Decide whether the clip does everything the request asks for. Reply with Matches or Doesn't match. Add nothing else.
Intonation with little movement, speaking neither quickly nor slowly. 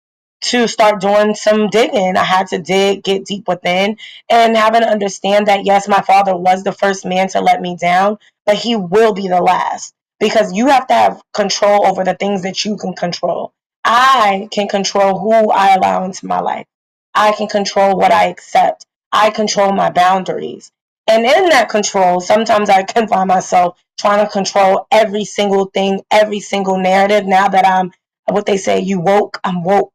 Matches